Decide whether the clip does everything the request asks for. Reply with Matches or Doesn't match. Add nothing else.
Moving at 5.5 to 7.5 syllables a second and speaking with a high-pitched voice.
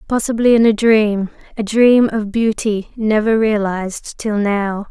Doesn't match